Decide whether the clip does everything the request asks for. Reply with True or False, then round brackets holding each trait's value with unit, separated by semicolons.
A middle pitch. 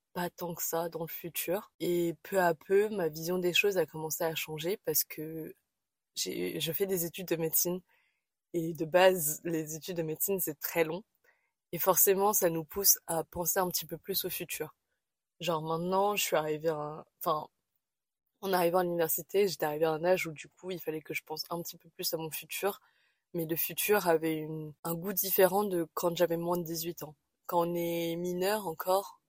True (170 Hz)